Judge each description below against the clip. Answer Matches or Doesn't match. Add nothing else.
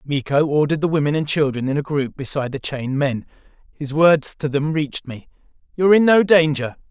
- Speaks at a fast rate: Matches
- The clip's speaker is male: Matches